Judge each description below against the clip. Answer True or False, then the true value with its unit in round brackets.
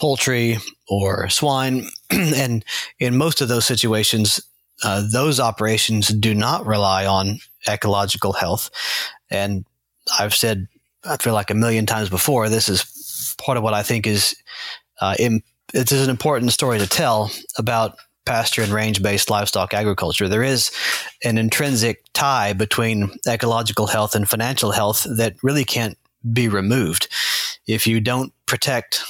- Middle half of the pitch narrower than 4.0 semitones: True (2.8 semitones)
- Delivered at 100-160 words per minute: True (145 wpm)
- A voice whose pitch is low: True (110 Hz)